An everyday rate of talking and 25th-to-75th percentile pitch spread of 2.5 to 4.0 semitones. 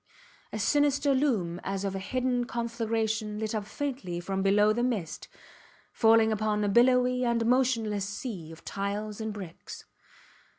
Yes: average, 145 wpm; average, 3.6 semitones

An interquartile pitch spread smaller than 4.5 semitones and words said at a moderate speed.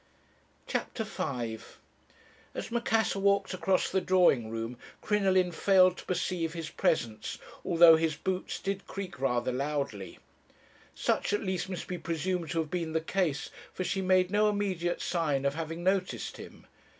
Yes: average, 4.0 semitones; average, 150 wpm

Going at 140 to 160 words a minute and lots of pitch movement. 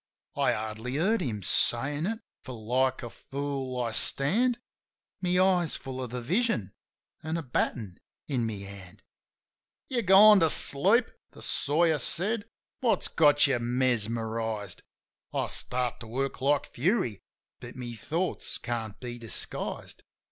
Yes: average, 145 wpm; wide, 6.4 semitones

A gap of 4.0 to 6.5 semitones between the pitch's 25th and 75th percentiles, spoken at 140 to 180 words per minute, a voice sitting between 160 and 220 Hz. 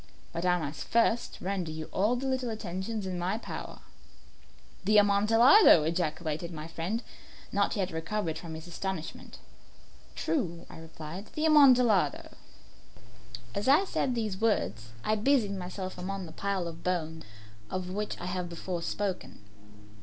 Yes: average, 4.3 semitones; average, 145 wpm; medium, 185 Hz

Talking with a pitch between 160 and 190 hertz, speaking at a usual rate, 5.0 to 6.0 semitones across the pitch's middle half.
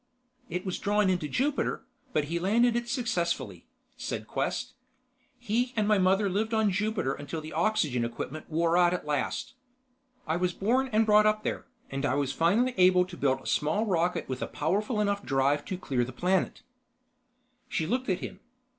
Yes: medium, 185 Hz; average, 180 wpm; wide, 5.4 semitones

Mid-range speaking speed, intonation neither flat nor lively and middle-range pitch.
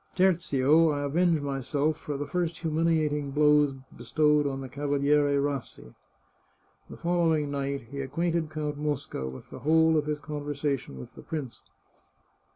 No: average, 145 wpm; narrow, 2.1 semitones; medium, 145 Hz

